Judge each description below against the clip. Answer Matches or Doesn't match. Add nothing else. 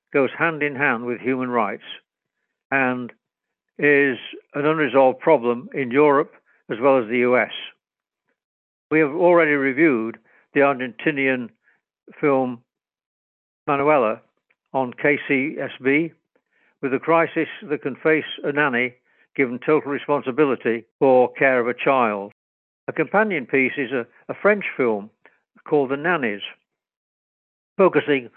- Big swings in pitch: Doesn't match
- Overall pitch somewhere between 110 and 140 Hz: Matches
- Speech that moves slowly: Matches